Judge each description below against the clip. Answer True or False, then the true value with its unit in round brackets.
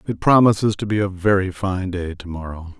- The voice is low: True (95 Hz)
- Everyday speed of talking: False (215 wpm)